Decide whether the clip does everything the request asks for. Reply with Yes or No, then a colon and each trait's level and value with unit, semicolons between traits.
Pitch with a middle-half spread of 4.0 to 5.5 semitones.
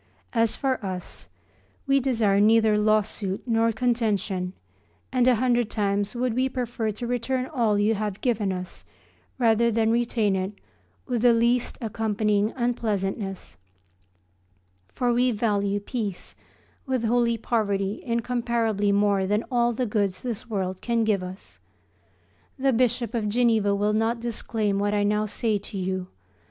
No: average, 2.8 semitones